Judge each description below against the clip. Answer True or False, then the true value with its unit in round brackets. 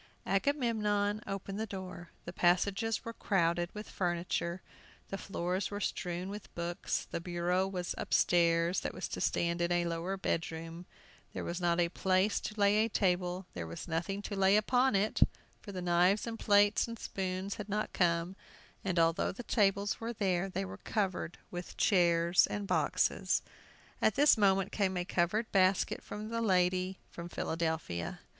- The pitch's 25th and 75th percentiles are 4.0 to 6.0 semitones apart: False (2.9 semitones)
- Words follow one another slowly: False (165 wpm)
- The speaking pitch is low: False (185 Hz)